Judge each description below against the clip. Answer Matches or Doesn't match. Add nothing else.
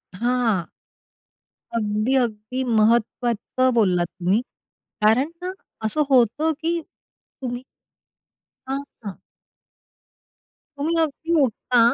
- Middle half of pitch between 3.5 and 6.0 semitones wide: Matches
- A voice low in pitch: Doesn't match